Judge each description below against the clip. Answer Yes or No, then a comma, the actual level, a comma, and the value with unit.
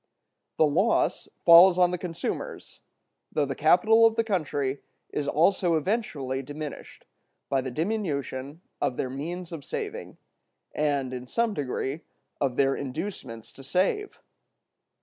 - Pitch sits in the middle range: Yes, medium, 155 Hz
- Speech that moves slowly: Yes, slow, 130 wpm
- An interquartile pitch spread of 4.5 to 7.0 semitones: Yes, average, 5.3 semitones